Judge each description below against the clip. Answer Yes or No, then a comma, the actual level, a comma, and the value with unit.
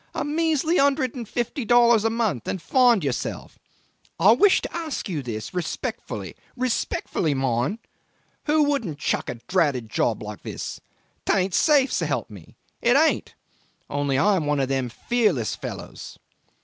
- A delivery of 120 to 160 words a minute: Yes, average, 150 wpm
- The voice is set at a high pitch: Yes, high, 215 Hz